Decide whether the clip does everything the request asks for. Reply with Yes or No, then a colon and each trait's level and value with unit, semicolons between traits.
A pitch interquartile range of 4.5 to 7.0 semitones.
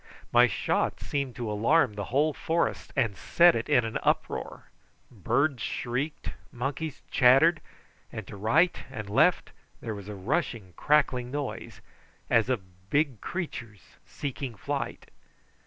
Yes: average, 5.1 semitones